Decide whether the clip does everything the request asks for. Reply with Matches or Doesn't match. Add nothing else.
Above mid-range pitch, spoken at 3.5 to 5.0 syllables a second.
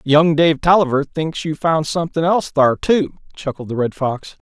Doesn't match